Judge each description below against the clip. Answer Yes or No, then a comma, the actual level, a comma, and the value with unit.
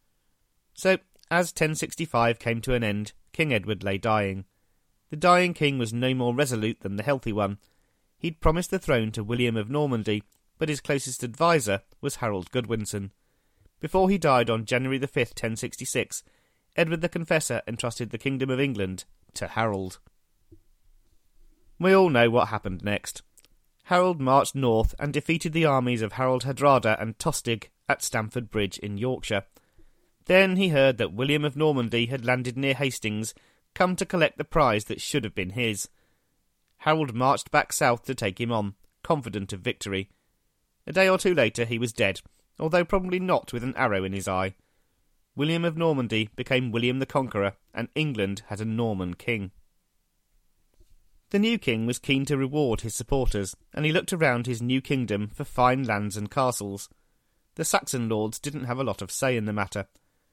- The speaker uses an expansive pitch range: Yes, wide, 5.9 semitones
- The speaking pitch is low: Yes, low, 120 Hz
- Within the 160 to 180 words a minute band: Yes, average, 175 wpm